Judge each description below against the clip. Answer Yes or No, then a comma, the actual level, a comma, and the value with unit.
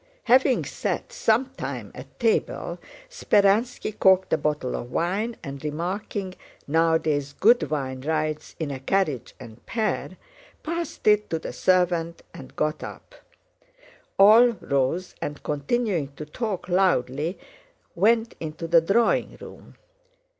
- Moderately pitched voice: Yes, medium, 175 Hz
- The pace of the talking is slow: Yes, slow, 125 wpm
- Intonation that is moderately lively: No, wide, 6.1 semitones